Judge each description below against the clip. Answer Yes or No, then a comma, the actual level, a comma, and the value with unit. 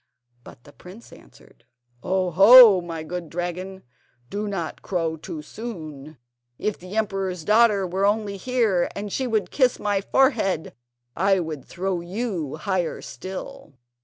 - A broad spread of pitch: No, average, 3.7 semitones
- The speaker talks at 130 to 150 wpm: Yes, average, 140 wpm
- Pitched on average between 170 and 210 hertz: Yes, high, 190 Hz